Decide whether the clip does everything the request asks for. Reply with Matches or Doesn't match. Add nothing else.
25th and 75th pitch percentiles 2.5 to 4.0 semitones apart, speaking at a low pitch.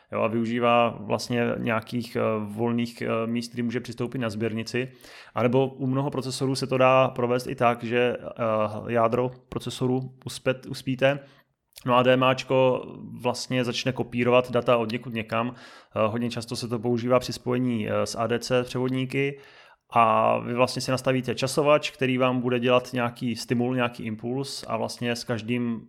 Doesn't match